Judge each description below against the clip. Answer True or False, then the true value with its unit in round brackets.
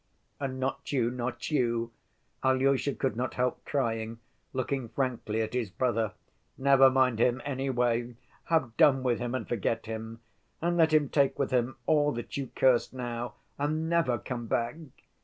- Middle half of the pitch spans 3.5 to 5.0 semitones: False (2.6 semitones)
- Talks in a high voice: False (125 Hz)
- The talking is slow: False (160 wpm)